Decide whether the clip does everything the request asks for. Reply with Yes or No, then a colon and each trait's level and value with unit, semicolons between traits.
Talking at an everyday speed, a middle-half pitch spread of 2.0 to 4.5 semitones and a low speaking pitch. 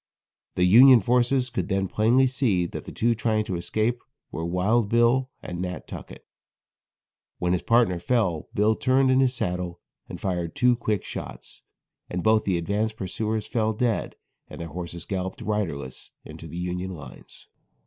No: average, 165 wpm; average, 4.9 semitones; low, 105 Hz